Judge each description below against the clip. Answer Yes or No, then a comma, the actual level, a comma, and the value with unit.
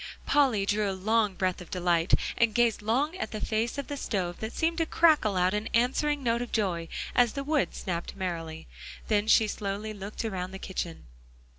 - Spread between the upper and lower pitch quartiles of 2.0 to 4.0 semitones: No, average, 4.5 semitones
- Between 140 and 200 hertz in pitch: No, high, 215 Hz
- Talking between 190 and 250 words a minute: Yes, average, 195 wpm